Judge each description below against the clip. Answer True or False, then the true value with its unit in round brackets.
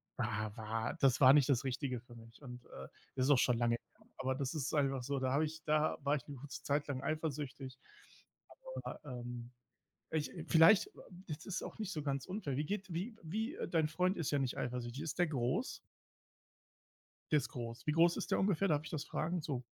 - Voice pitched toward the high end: False (145 Hz)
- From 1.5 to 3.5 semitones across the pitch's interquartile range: False (4.2 semitones)